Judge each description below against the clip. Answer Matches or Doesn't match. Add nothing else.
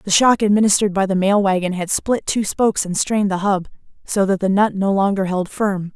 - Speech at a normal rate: Doesn't match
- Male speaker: Doesn't match